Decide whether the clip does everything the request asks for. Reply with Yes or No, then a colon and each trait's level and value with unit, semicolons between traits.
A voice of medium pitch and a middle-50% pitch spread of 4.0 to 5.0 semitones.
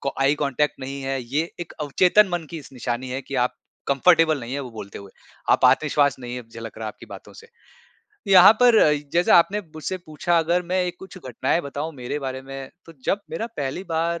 Yes: medium, 145 Hz; average, 4.6 semitones